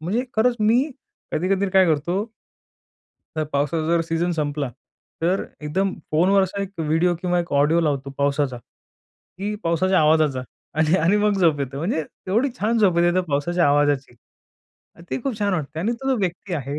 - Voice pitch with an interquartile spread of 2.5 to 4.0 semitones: No, average, 4.5 semitones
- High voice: No, medium, 170 Hz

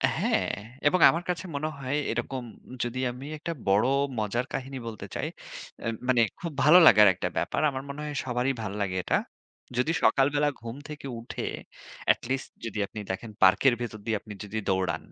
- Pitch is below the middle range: Yes, low, 125 Hz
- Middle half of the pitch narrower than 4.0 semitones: No, average, 4.6 semitones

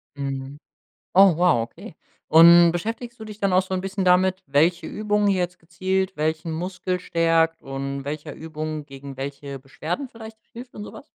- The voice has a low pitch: No, medium, 170 Hz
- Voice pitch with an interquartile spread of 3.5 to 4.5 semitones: Yes, average, 4.2 semitones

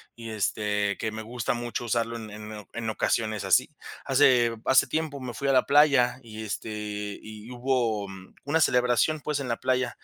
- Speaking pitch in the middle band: No, low, 115 Hz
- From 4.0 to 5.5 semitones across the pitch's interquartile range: No, average, 3.0 semitones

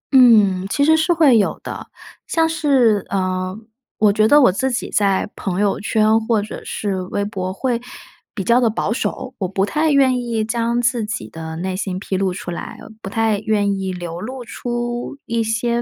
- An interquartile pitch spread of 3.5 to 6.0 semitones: Yes, average, 3.9 semitones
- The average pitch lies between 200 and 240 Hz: Yes, high, 215 Hz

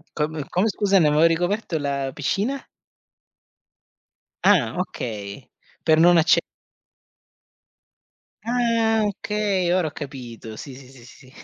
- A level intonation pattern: No, wide, 6.7 semitones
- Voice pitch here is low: No, medium, 165 Hz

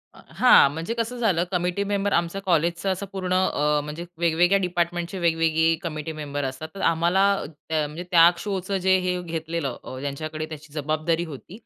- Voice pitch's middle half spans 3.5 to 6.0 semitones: No, average, 2.9 semitones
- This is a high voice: No, medium, 170 Hz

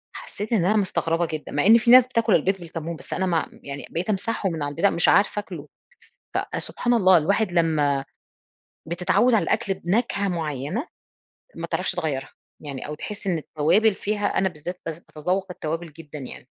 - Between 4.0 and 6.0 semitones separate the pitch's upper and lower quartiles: Yes, average, 4.7 semitones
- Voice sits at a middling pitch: Yes, medium, 175 Hz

